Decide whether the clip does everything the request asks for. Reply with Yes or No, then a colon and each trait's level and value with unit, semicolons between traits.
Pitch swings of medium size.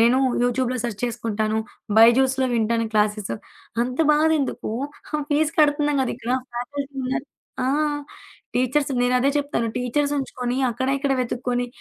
Yes: average, 3.1 semitones